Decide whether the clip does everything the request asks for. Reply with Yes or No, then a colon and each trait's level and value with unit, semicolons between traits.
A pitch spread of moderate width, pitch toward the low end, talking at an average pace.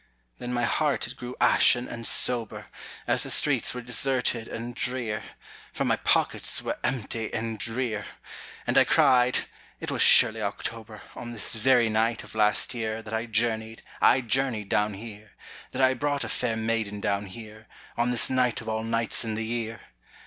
No: narrow, 2.0 semitones; low, 115 Hz; average, 180 wpm